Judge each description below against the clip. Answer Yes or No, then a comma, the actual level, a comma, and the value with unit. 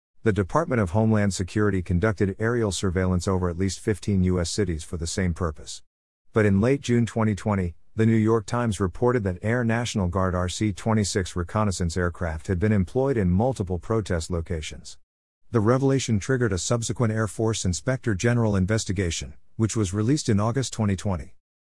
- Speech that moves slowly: No, average, 165 wpm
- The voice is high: No, low, 100 Hz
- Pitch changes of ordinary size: Yes, average, 3.8 semitones